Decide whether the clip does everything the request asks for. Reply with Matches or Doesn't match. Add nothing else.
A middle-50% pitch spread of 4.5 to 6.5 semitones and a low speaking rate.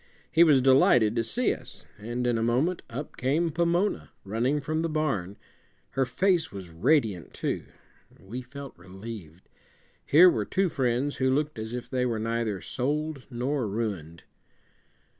Doesn't match